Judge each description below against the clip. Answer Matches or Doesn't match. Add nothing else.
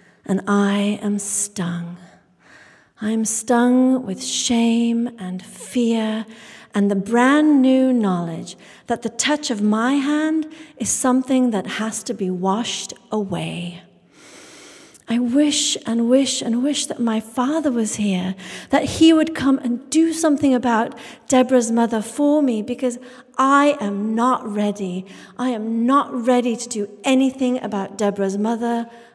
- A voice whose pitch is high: Matches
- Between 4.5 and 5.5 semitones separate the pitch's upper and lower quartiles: Doesn't match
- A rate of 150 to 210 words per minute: Doesn't match